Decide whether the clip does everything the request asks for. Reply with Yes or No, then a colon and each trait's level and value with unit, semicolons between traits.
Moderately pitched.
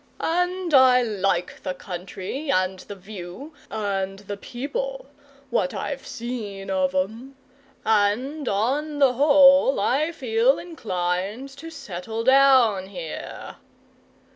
No: high, 230 Hz